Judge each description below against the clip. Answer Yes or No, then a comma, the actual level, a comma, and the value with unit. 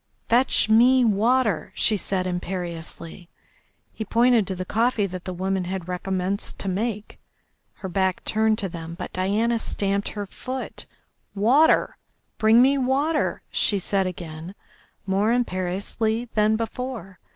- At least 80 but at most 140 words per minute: Yes, slow, 135 wpm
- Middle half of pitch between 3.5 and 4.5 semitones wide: Yes, average, 3.8 semitones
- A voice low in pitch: No, high, 200 Hz